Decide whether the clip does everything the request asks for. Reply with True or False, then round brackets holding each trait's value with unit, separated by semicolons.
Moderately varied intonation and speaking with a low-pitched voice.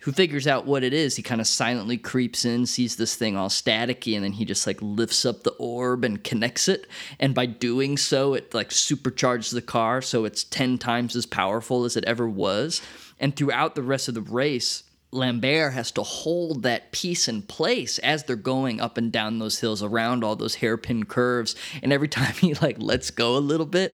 True (3.2 semitones; 125 Hz)